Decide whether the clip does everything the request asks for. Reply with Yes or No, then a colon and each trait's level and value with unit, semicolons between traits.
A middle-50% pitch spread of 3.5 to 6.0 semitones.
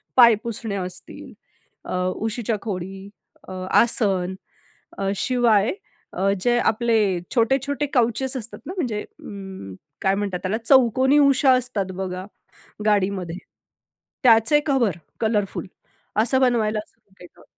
Yes: average, 4.3 semitones